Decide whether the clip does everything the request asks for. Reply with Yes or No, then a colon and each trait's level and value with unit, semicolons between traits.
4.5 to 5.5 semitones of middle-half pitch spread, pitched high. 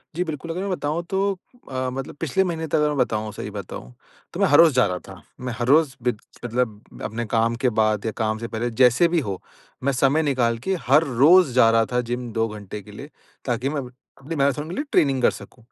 No: average, 4.9 semitones; low, 125 Hz